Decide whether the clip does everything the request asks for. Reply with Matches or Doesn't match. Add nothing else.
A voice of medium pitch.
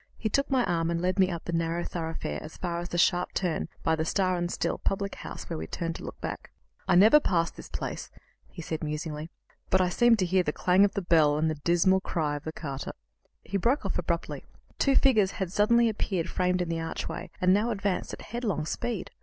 Matches